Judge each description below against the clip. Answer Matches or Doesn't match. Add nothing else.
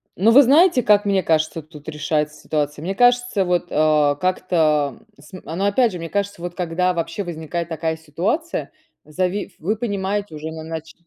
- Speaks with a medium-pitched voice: Matches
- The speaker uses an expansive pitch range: Doesn't match